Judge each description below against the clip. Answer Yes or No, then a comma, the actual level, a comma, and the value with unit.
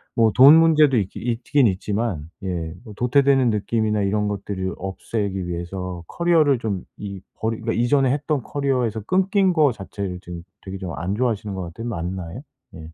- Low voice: Yes, low, 105 Hz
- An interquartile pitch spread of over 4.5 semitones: Yes, wide, 5.5 semitones